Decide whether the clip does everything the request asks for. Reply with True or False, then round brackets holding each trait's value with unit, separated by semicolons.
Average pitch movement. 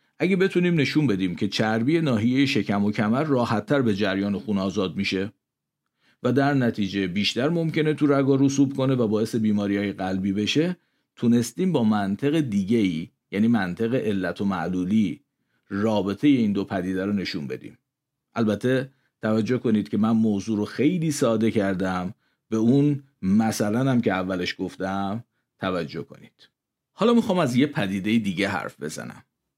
False (5.7 semitones)